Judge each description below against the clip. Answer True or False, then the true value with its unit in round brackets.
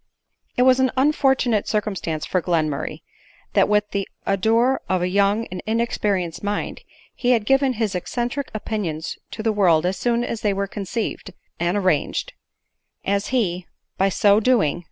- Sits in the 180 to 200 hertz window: False (210 Hz)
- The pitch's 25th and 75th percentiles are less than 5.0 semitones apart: True (4.2 semitones)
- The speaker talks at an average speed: True (165 wpm)